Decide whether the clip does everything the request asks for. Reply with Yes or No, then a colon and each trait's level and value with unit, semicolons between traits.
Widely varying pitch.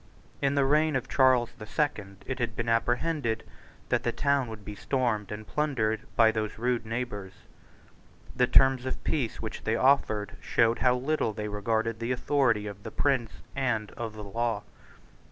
No: average, 3.5 semitones